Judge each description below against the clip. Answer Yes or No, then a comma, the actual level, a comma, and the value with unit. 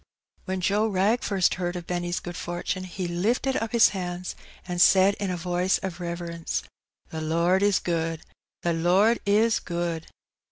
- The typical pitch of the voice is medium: Yes, medium, 180 Hz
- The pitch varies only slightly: Yes, narrow, 2.3 semitones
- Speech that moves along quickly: No, average, 175 wpm